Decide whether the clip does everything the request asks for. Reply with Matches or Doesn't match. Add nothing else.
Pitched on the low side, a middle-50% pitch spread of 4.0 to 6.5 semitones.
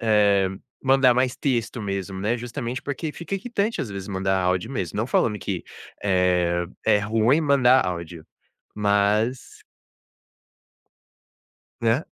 Matches